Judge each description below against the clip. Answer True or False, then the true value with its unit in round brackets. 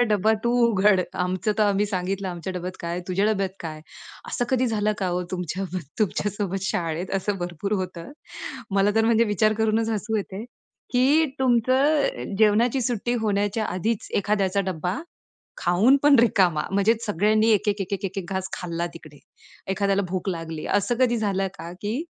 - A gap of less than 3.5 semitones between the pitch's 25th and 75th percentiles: True (3.1 semitones)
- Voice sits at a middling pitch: False (200 Hz)